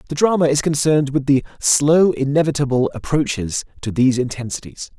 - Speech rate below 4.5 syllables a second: No, 5.7 syllables/s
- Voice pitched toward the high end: No, medium, 140 Hz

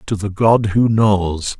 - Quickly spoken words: No, average, 190 wpm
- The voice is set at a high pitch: No, low, 100 Hz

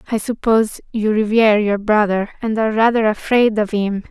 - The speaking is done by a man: No, female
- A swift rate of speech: No, average, 175 wpm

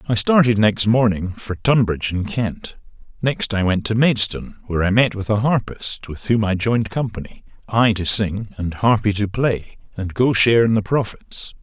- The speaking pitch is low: Yes, low, 105 Hz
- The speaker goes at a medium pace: Yes, average, 190 wpm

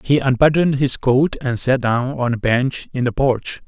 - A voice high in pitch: No, low, 130 Hz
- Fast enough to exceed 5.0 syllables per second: No, 4.6 syllables/s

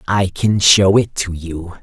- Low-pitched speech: Yes, very low, 95 Hz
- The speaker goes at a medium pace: Yes, average, 195 wpm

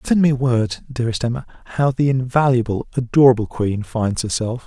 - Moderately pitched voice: No, low, 125 Hz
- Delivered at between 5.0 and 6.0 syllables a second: Yes, 5.4 syllables/s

